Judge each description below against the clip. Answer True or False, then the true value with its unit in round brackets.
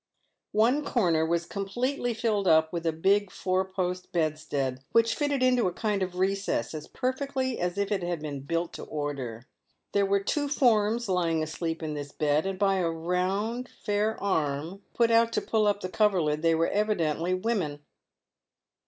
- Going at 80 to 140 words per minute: False (175 wpm)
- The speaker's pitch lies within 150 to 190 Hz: True (185 Hz)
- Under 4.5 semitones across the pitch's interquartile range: False (5.1 semitones)